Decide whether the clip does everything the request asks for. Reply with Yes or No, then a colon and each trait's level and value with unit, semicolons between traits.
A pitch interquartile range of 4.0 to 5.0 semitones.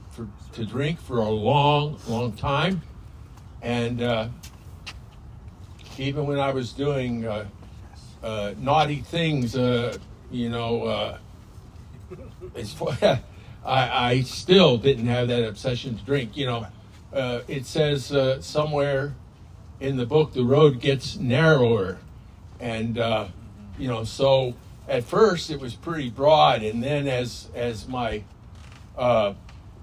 Yes: average, 4.5 semitones